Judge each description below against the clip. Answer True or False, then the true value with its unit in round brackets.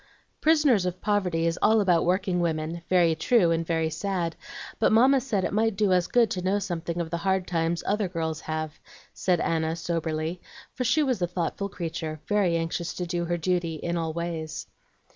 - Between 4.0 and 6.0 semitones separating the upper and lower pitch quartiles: False (3.0 semitones)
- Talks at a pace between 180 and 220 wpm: True (190 wpm)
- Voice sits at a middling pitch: True (175 Hz)